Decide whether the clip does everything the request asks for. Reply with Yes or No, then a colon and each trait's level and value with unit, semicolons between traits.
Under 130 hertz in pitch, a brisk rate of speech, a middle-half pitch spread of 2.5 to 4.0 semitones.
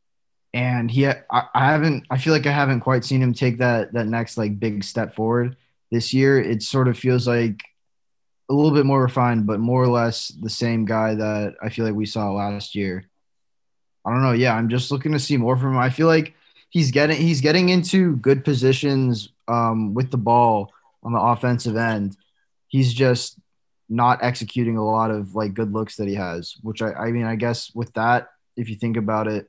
Yes: low, 120 Hz; fast, 210 wpm; average, 3.0 semitones